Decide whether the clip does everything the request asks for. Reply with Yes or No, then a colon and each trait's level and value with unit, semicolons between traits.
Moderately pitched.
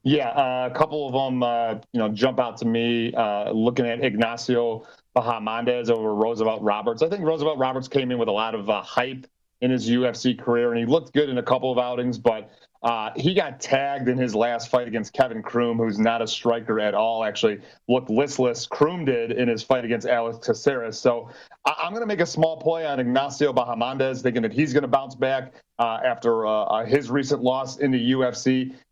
No: low, 125 Hz